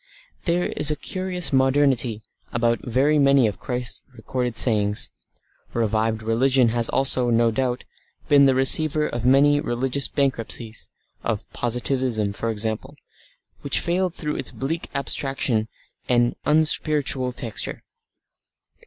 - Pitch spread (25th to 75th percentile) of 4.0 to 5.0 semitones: No, average, 3.5 semitones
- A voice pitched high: No, low, 130 Hz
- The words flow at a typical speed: No, slow, 125 wpm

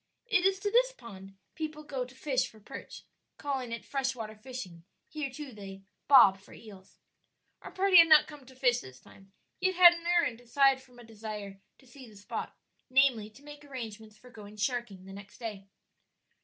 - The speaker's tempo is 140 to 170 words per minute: No, average, 195 wpm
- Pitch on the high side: Yes, very high, 250 Hz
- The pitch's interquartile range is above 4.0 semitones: Yes, wide, 5.4 semitones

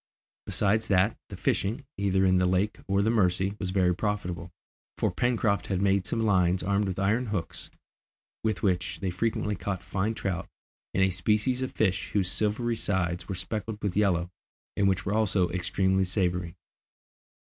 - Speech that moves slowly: No, average, 170 wpm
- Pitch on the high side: No, very low, 95 Hz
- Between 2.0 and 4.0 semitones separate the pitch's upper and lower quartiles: Yes, narrow, 2.4 semitones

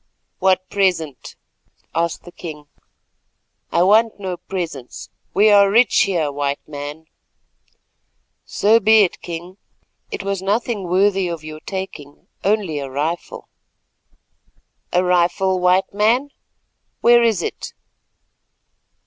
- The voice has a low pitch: No, medium, 185 Hz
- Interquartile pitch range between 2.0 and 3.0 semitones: No, average, 3.7 semitones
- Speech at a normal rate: No, slow, 115 wpm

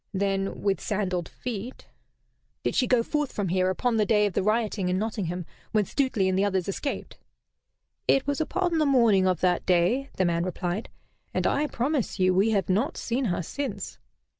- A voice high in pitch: Yes, high, 205 Hz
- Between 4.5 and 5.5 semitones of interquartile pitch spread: Yes, average, 5.1 semitones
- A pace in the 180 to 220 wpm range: Yes, average, 190 wpm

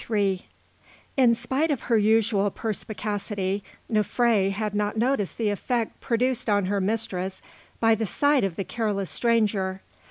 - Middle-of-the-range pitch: No, high, 215 Hz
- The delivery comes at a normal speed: Yes, average, 145 wpm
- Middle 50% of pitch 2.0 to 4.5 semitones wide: Yes, average, 2.7 semitones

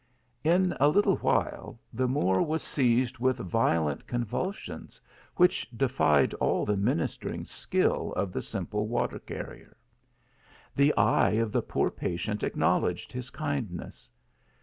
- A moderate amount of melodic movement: No, wide, 6.1 semitones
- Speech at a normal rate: No, slow, 130 wpm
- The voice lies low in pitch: Yes, low, 120 Hz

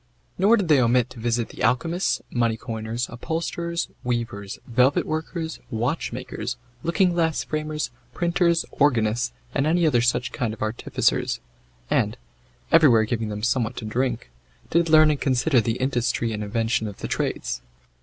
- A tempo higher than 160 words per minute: No, average, 145 wpm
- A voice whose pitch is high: No, low, 125 Hz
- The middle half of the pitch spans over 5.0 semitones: Yes, wide, 5.6 semitones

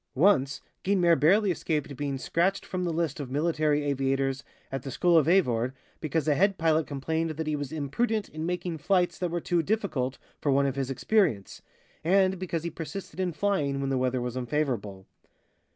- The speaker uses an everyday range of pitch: Yes, average, 4.5 semitones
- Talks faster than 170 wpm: Yes, average, 185 wpm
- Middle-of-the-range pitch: Yes, medium, 155 Hz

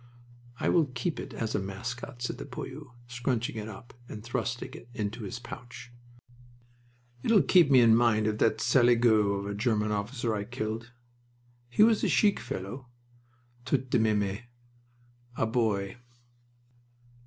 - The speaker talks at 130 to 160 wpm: Yes, average, 150 wpm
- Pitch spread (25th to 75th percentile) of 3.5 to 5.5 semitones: No, average, 2.8 semitones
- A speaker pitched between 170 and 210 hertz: No, low, 115 Hz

